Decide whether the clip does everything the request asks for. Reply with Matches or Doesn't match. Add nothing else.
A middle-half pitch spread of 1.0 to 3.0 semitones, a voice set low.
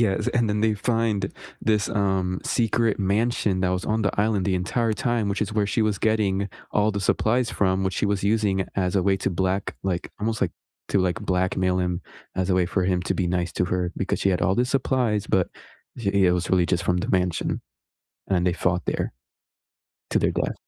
Matches